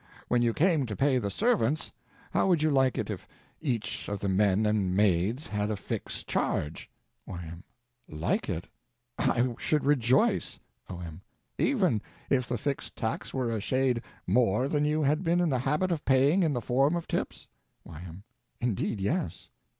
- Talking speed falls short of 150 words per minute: No, average, 170 wpm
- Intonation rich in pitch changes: Yes, wide, 6.4 semitones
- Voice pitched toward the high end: No, low, 125 Hz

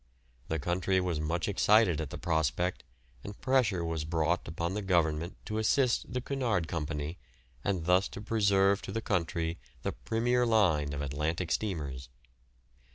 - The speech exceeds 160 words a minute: No, average, 155 wpm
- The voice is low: Yes, very low, 90 Hz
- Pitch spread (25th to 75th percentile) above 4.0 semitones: Yes, average, 4.5 semitones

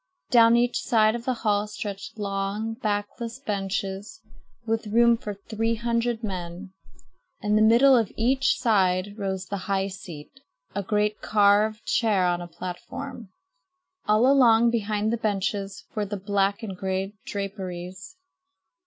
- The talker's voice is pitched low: No, high, 210 Hz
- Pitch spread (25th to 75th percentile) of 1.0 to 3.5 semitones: Yes, average, 2.8 semitones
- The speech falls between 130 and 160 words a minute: Yes, average, 140 wpm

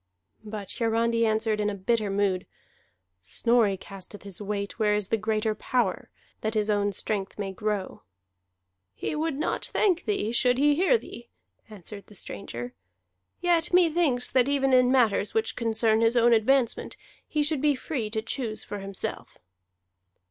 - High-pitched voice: Yes, high, 225 Hz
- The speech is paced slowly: No, average, 155 wpm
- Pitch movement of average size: Yes, average, 3.7 semitones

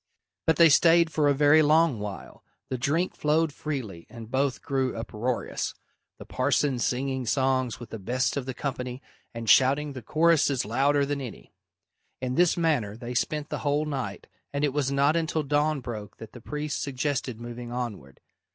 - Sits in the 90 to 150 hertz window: Yes, low, 135 Hz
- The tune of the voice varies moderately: Yes, average, 3.5 semitones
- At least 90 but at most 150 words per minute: No, average, 175 wpm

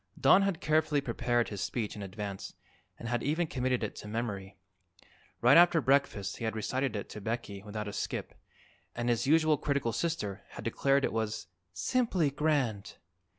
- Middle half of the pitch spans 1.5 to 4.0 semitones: No, wide, 5.6 semitones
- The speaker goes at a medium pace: Yes, average, 170 wpm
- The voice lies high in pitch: No, low, 120 Hz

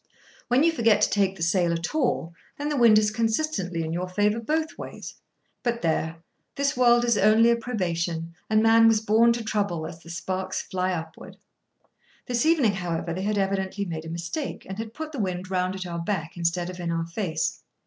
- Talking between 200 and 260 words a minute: Yes, fast, 205 wpm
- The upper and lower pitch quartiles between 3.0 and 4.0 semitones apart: No, average, 5.1 semitones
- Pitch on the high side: Yes, high, 195 Hz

